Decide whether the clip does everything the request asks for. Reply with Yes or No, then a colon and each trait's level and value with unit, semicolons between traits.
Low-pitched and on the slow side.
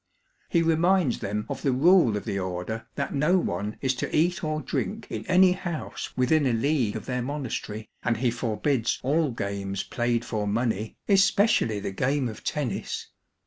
No: low, 125 Hz; average, 180 wpm